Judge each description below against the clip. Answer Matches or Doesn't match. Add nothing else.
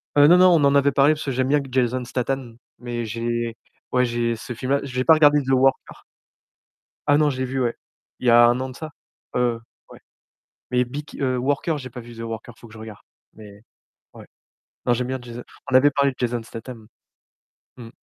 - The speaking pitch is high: Doesn't match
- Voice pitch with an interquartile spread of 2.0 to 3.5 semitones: Matches